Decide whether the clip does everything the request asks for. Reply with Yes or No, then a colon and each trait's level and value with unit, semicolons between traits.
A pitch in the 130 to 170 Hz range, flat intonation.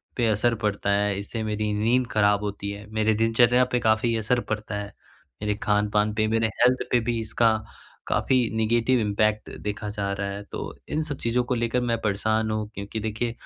No: low, 110 Hz; narrow, 2.1 semitones